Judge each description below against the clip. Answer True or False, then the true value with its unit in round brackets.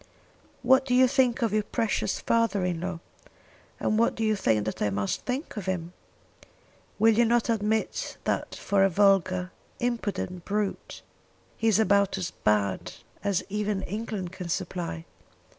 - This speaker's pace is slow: False (160 wpm)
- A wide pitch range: False (3.7 semitones)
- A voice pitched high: True (200 Hz)